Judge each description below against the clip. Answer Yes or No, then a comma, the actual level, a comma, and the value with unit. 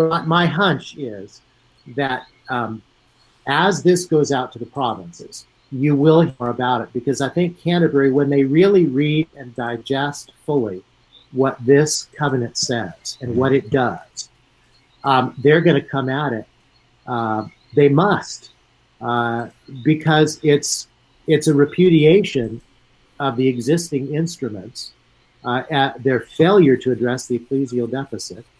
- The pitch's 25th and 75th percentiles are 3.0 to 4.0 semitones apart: Yes, average, 3.4 semitones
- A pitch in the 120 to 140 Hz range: Yes, low, 130 Hz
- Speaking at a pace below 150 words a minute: Yes, average, 140 wpm